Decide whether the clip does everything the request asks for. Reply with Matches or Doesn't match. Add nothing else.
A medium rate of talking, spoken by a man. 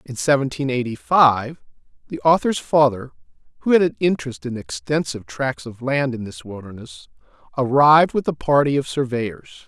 Matches